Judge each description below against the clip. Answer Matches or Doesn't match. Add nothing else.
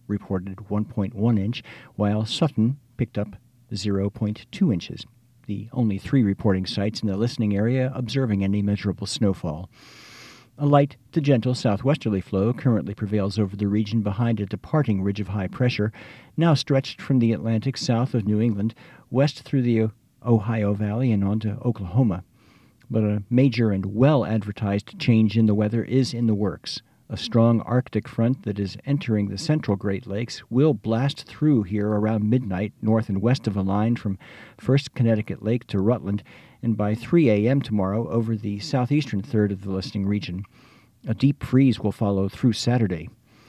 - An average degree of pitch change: Matches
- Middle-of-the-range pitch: Doesn't match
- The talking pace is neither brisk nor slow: Matches